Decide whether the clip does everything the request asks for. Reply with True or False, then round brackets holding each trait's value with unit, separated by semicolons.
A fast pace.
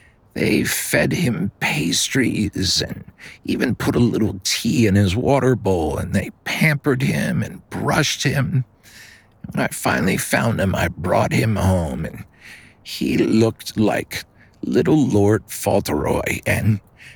False (135 wpm)